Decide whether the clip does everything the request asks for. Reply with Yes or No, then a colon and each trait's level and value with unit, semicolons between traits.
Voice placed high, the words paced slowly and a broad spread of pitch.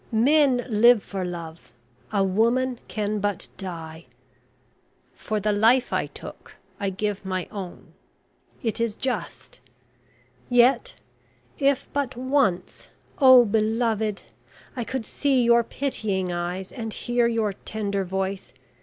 No: high, 215 Hz; slow, 120 wpm; average, 4.2 semitones